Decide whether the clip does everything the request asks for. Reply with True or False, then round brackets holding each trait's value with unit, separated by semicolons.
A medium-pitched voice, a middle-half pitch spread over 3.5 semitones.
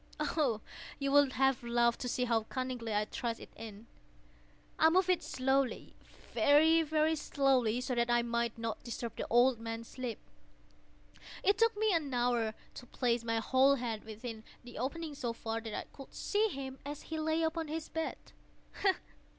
False (255 Hz; 4.5 semitones)